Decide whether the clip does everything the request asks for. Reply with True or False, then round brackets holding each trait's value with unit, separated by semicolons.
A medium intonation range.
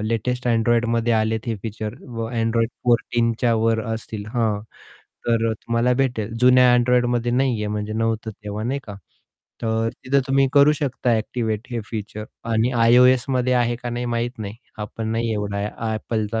False (1.9 semitones)